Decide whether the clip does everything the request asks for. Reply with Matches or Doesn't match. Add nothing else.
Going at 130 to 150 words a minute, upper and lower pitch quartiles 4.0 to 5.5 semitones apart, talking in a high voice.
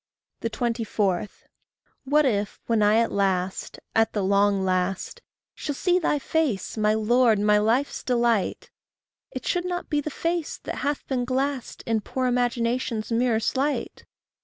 Matches